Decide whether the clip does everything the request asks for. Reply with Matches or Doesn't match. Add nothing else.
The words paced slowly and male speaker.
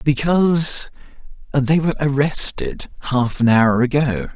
Matches